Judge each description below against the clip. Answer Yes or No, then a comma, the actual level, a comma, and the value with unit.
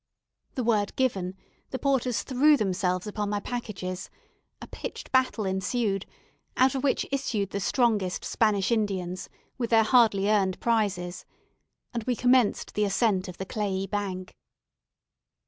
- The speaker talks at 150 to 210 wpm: No, average, 140 wpm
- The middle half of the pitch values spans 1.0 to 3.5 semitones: No, average, 4.1 semitones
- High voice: Yes, high, 210 Hz